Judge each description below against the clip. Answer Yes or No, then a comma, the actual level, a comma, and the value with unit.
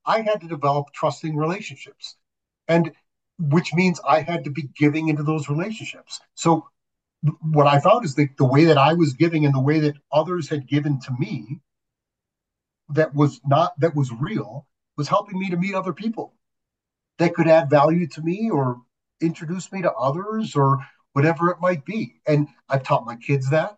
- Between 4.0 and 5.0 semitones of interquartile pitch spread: No, average, 3.0 semitones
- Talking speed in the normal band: Yes, average, 185 wpm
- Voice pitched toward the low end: No, medium, 155 Hz